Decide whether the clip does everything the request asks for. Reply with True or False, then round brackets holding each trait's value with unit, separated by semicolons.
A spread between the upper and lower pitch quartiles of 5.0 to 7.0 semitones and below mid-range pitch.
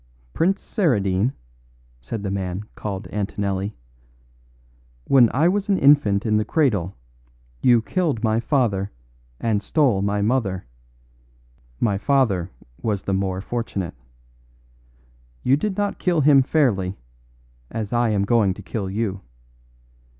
True (5.6 semitones; 110 Hz)